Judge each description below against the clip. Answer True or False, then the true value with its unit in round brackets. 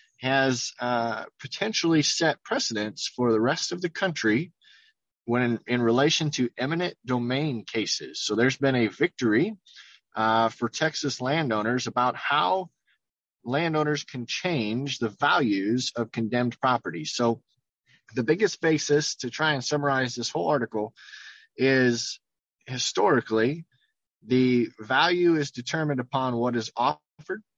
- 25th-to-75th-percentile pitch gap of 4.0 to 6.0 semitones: True (4.4 semitones)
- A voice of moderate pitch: False (130 Hz)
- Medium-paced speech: False (130 wpm)